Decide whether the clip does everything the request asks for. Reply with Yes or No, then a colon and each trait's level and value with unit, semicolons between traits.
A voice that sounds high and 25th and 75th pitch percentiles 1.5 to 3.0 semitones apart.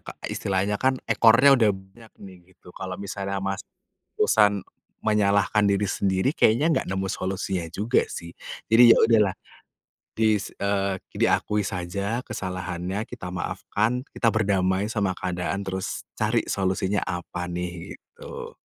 No: low, 100 Hz; average, 2.7 semitones